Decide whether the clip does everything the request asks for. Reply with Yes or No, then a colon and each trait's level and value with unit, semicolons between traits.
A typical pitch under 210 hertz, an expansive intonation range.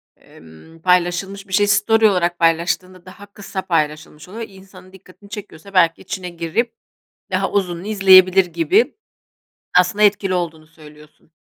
No: medium, 185 Hz; average, 2.8 semitones